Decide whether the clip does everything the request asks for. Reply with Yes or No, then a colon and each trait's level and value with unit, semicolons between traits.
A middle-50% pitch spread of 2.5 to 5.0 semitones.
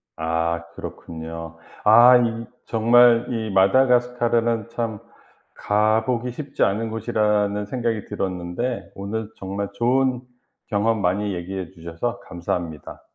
Yes: average, 3.8 semitones